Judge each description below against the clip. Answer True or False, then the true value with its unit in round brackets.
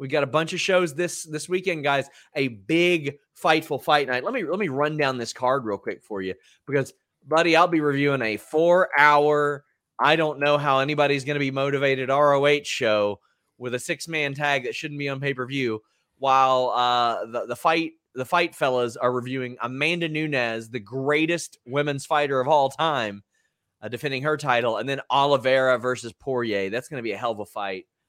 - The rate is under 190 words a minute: False (205 wpm)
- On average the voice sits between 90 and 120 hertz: False (140 Hz)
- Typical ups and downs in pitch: True (3.3 semitones)